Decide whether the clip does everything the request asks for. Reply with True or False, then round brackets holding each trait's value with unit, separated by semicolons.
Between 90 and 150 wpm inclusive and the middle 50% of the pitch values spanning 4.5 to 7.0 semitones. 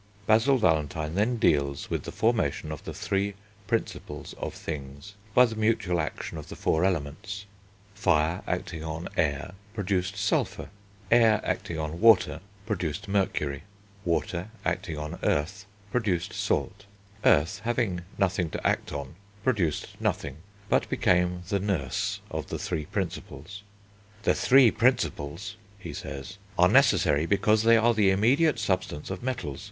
True (140 wpm; 5.4 semitones)